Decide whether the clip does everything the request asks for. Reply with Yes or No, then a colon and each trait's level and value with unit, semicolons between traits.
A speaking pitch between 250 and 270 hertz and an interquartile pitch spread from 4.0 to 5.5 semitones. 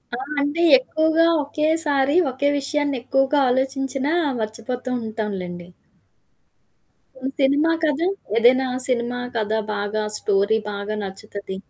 Yes: very high, 260 Hz; average, 5.0 semitones